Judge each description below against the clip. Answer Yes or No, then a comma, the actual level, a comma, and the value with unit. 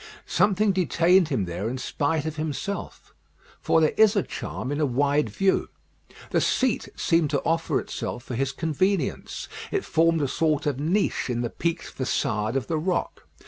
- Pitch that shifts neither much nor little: Yes, average, 4.6 semitones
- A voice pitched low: No, medium, 155 Hz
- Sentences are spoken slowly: No, average, 175 wpm